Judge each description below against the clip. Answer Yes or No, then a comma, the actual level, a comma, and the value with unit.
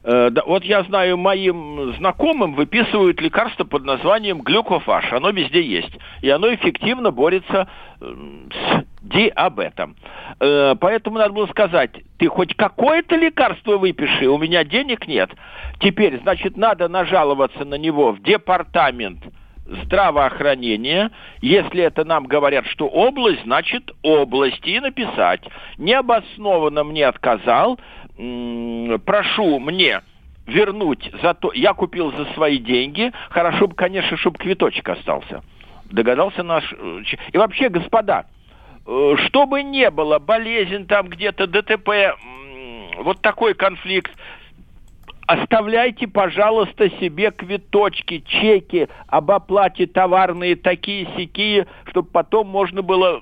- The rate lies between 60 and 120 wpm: Yes, slow, 110 wpm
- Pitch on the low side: No, high, 190 Hz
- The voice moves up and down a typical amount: Yes, average, 4.8 semitones